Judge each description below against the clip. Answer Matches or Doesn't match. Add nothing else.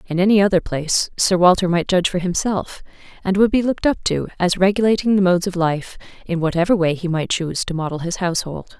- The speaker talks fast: Matches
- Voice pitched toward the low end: Doesn't match